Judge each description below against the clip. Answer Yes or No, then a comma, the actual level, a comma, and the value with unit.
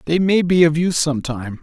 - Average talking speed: No, fast, 260 wpm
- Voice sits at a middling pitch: Yes, medium, 160 Hz